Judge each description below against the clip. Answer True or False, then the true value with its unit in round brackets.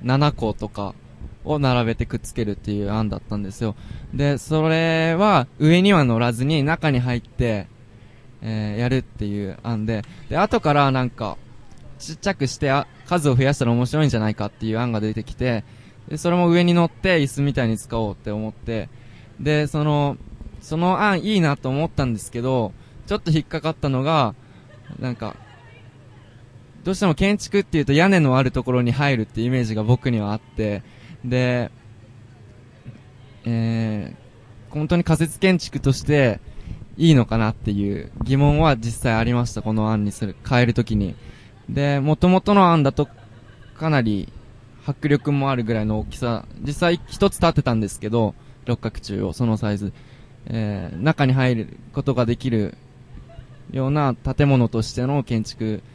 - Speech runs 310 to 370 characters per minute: True (315 characters per minute)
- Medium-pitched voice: False (125 Hz)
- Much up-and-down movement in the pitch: False (4.4 semitones)